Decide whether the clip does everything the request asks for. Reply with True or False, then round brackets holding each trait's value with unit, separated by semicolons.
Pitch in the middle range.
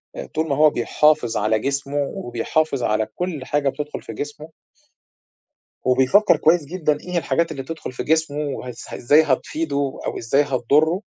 True (145 Hz)